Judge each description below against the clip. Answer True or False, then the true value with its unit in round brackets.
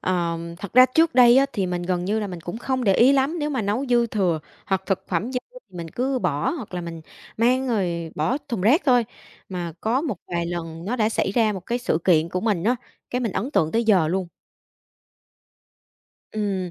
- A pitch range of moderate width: False (5.9 semitones)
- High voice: True (205 Hz)